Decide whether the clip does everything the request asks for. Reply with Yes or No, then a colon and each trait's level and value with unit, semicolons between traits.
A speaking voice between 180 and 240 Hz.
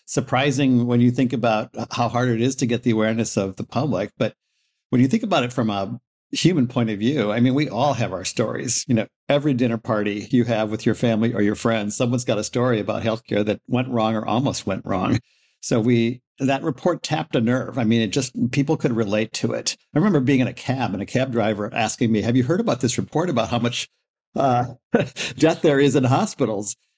No: low, 120 Hz